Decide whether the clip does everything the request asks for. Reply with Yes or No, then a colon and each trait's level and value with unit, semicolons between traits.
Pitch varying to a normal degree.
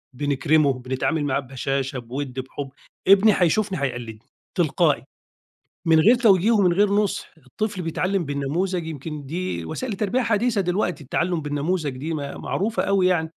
No: wide, 5.8 semitones